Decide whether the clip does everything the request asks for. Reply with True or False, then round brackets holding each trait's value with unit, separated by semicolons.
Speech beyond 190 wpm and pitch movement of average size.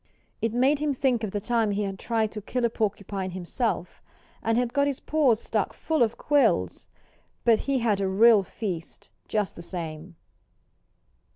False (175 wpm; 4.1 semitones)